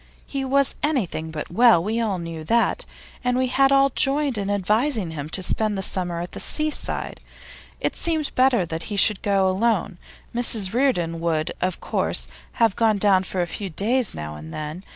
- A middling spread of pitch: No, wide, 6.2 semitones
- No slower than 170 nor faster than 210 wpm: Yes, average, 190 wpm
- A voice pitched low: No, high, 205 Hz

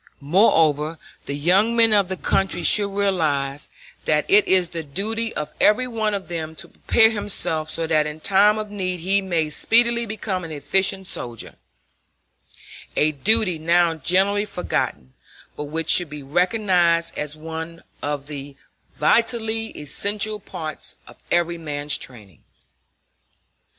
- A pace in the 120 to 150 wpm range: Yes, average, 140 wpm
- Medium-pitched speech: Yes, medium, 175 Hz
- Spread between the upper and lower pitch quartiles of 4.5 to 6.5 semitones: Yes, average, 5.1 semitones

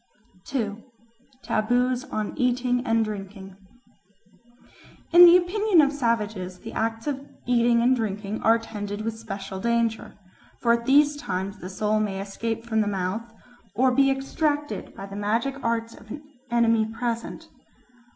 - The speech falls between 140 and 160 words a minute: Yes, average, 145 wpm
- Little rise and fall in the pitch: No, average, 3.3 semitones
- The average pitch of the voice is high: Yes, high, 230 Hz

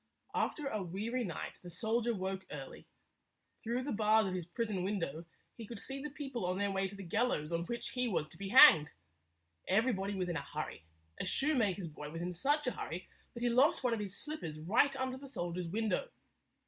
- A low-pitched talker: No, high, 205 Hz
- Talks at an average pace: No, fast, 210 wpm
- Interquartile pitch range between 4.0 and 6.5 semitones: Yes, wide, 5.6 semitones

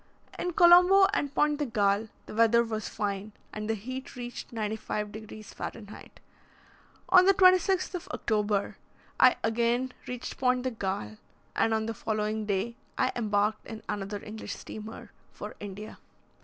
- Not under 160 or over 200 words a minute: No, average, 150 wpm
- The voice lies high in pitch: Yes, high, 220 Hz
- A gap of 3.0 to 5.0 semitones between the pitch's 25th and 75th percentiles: Yes, average, 3.4 semitones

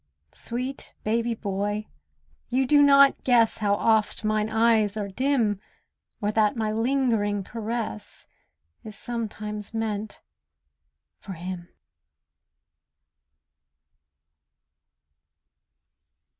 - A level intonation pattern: Yes, narrow, 2.3 semitones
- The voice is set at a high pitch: Yes, high, 220 Hz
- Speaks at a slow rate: Yes, slow, 85 wpm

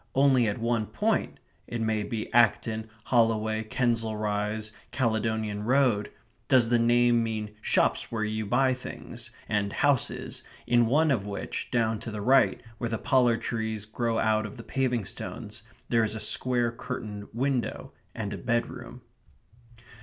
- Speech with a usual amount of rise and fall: No, narrow, 2.0 semitones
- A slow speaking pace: No, average, 155 wpm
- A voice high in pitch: No, low, 115 Hz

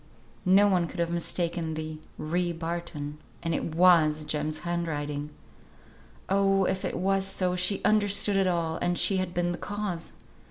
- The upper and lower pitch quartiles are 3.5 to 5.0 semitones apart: No, average, 2.9 semitones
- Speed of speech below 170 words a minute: Yes, average, 160 wpm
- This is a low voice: No, medium, 175 Hz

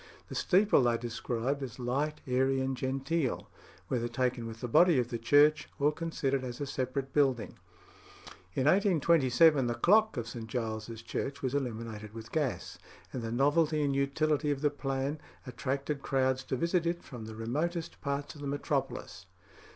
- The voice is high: No, low, 135 Hz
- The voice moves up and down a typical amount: Yes, average, 3.5 semitones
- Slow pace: No, average, 165 wpm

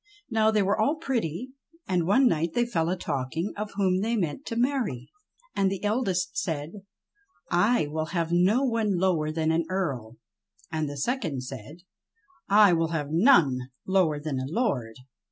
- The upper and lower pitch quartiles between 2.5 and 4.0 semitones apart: No, wide, 5.5 semitones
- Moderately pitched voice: Yes, medium, 180 Hz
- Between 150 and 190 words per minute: Yes, average, 170 wpm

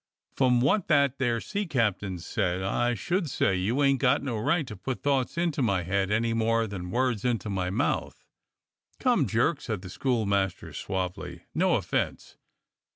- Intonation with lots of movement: Yes, wide, 6.0 semitones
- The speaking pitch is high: No, low, 115 Hz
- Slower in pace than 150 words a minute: No, average, 165 wpm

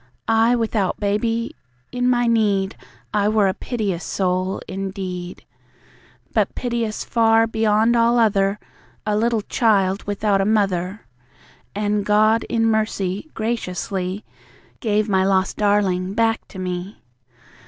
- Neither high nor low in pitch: No, high, 210 Hz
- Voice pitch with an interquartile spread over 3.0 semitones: No, average, 2.7 semitones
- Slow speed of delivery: Yes, slow, 120 wpm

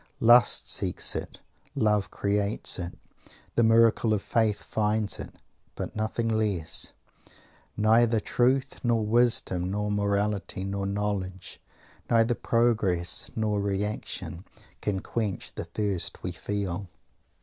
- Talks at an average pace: No, slow, 115 wpm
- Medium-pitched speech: No, low, 105 Hz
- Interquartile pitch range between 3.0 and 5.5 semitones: No, narrow, 2.4 semitones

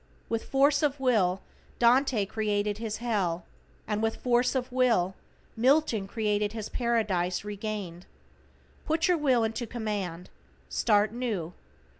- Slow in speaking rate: Yes, slow, 125 wpm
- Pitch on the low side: No, high, 220 Hz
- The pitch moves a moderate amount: Yes, average, 3.4 semitones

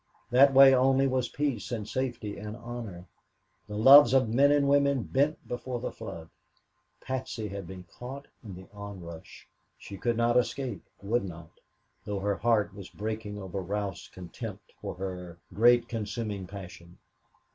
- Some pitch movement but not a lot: Yes, average, 4.8 semitones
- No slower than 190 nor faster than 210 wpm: No, average, 155 wpm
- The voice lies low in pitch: Yes, low, 110 Hz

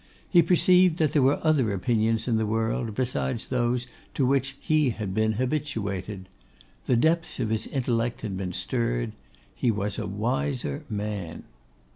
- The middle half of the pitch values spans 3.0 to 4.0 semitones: No, average, 4.4 semitones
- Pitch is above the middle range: No, low, 120 Hz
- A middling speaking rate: Yes, average, 155 wpm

